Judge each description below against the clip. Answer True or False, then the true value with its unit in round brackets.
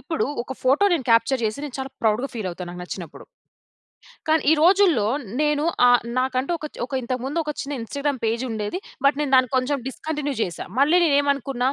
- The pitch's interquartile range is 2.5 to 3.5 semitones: False (4.1 semitones)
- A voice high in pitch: True (265 Hz)